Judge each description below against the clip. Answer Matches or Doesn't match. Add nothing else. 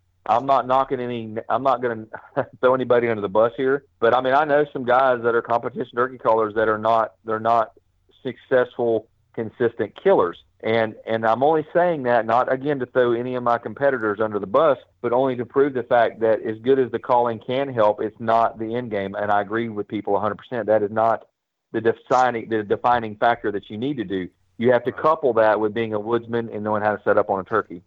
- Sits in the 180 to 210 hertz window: Doesn't match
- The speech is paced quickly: Matches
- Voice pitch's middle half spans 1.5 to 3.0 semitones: Matches